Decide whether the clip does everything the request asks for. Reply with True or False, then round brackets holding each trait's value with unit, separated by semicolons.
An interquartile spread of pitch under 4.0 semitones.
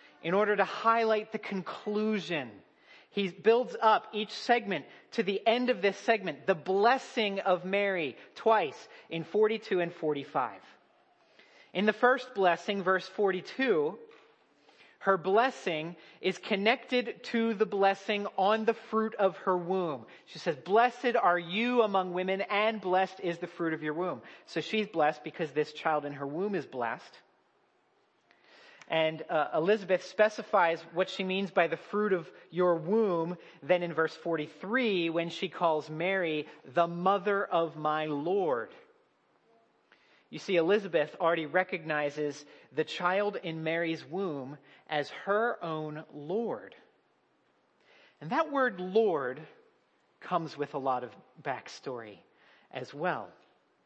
False (4.8 semitones)